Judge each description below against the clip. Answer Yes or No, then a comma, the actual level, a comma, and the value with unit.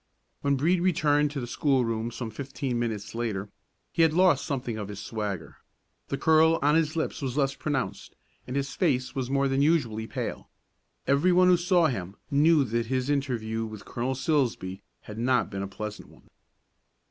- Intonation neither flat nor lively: Yes, average, 4.8 semitones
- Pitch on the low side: Yes, low, 130 Hz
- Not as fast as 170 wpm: No, average, 180 wpm